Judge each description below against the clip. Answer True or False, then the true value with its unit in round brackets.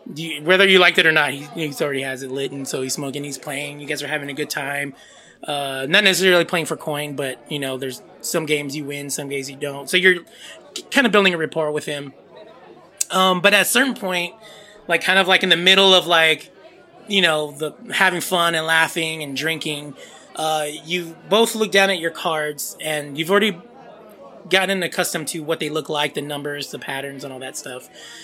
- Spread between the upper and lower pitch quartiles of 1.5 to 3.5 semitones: False (4.3 semitones)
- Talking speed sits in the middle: False (220 wpm)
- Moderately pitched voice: True (160 Hz)